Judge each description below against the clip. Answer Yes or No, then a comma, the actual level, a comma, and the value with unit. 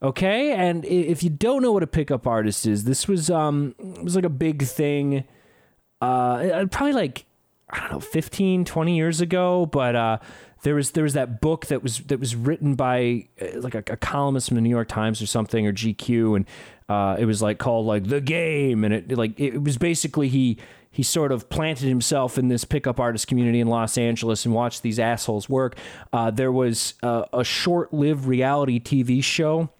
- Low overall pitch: Yes, low, 130 Hz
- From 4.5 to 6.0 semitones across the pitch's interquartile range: Yes, average, 5.2 semitones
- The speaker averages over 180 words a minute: Yes, fast, 205 wpm